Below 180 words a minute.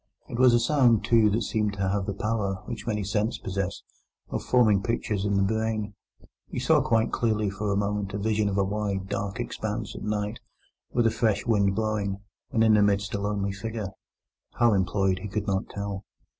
No: average, 200 wpm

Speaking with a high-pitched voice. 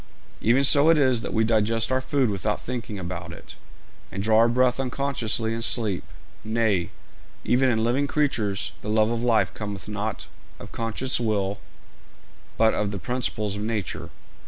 No: low, 115 Hz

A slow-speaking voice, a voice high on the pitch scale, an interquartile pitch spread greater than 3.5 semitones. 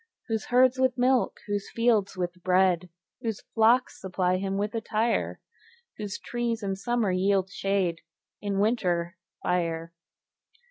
Yes: slow, 130 wpm; high, 200 Hz; average, 4.0 semitones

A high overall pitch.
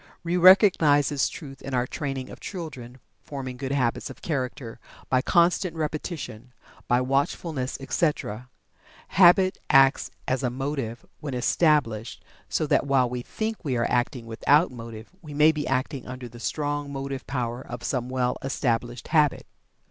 No: low, 135 Hz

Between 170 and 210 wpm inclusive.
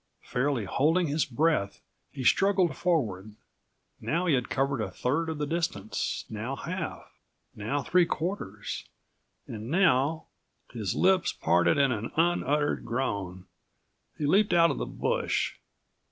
No: slow, 135 wpm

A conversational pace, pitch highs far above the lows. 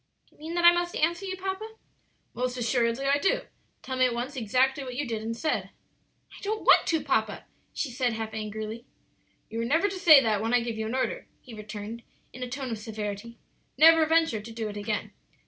No: fast, 220 wpm; wide, 5.9 semitones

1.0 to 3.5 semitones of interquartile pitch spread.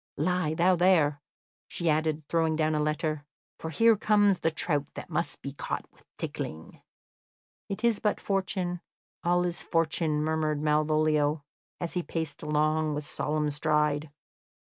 Yes: average, 2.7 semitones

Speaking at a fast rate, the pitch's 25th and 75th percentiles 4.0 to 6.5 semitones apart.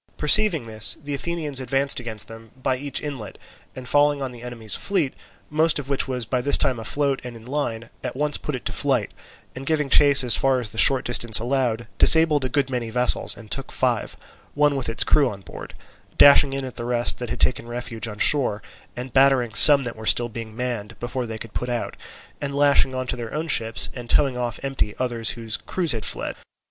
No: fast, 220 wpm; average, 3.2 semitones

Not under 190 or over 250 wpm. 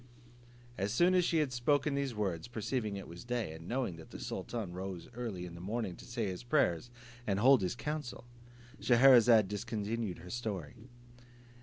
No: average, 175 wpm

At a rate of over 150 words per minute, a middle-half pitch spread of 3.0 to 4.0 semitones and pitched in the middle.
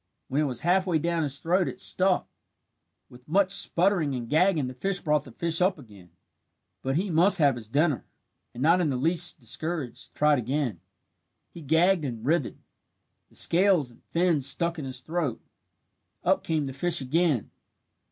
No: average, 175 wpm; average, 4.8 semitones; medium, 155 Hz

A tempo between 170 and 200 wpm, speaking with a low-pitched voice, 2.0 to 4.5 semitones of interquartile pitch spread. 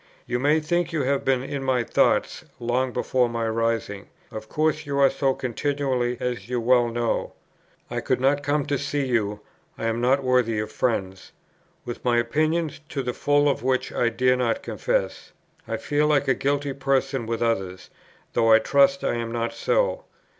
Yes: average, 185 wpm; low, 130 Hz; average, 3.3 semitones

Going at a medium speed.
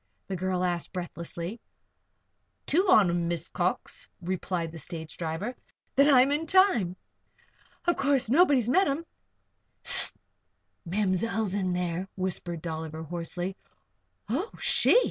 No: slow, 125 wpm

